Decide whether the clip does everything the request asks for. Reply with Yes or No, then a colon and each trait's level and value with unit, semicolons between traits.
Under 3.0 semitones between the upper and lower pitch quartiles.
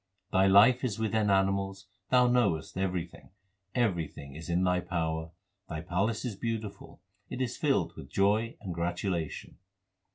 No: average, 4.2 semitones